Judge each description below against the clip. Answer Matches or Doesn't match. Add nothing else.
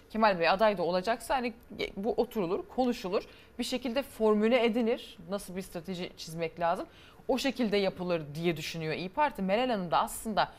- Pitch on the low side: Doesn't match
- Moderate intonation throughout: Matches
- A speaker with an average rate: Doesn't match